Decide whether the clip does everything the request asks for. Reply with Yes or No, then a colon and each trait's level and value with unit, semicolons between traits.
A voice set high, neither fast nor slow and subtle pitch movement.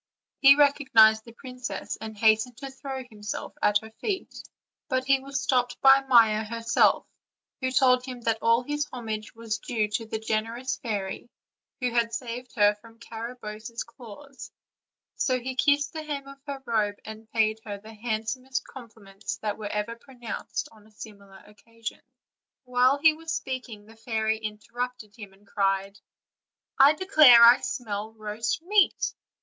No: high, 230 Hz; average, 155 wpm; average, 3.2 semitones